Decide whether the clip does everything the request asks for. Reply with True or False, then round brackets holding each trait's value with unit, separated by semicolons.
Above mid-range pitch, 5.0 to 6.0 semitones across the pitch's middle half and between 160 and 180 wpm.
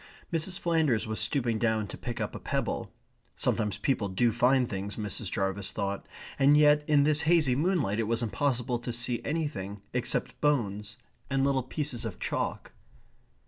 False (120 Hz; 5.3 semitones; 165 wpm)